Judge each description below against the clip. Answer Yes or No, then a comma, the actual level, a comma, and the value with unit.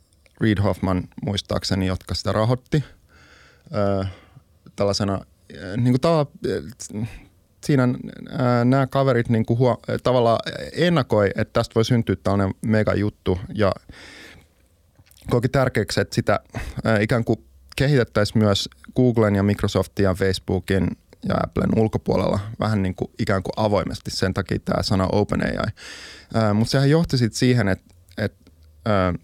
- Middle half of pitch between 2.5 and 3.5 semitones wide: No, average, 4.2 semitones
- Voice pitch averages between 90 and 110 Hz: Yes, low, 105 Hz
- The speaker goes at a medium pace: Yes, average, 140 wpm